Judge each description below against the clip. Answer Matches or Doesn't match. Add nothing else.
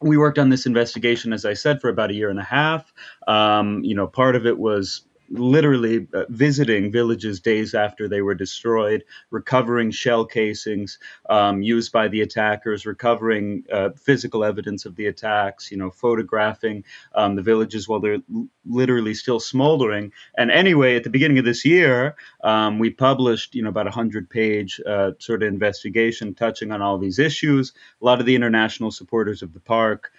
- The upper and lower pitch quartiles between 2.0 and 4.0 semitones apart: Matches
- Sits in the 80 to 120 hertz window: Matches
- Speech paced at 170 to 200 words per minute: Matches